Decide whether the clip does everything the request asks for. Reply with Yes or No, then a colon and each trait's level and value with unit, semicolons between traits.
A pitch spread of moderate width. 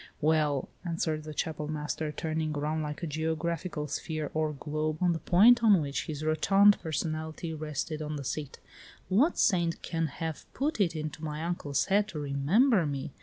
No: narrow, 2.0 semitones